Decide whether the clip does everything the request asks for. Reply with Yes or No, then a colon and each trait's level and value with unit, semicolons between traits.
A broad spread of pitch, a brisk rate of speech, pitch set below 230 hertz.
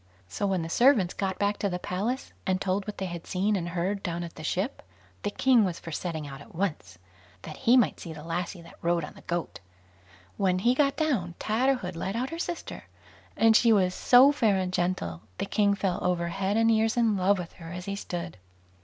No: average, 4.1 semitones; fast, 225 wpm; high, 190 Hz